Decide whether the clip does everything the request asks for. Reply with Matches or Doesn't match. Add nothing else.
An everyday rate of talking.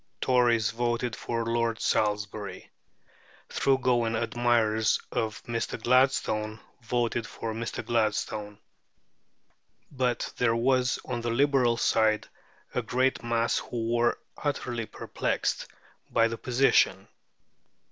Doesn't match